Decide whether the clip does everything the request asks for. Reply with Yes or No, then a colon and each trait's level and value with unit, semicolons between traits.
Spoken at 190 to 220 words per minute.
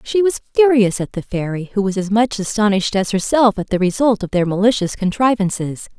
Yes: average, 200 wpm